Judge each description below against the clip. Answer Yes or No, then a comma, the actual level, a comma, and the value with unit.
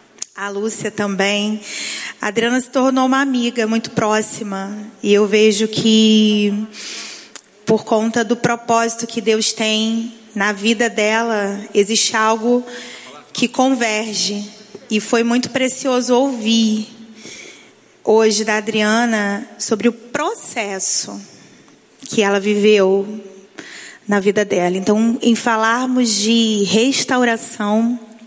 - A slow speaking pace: Yes, slow, 110 wpm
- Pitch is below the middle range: No, high, 220 Hz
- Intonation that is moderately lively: No, narrow, 1.9 semitones